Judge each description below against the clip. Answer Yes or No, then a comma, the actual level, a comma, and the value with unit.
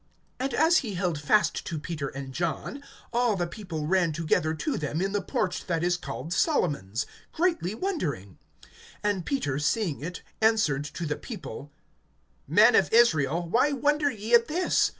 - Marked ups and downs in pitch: Yes, wide, 7.6 semitones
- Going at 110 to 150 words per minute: No, average, 165 wpm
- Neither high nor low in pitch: Yes, medium, 180 Hz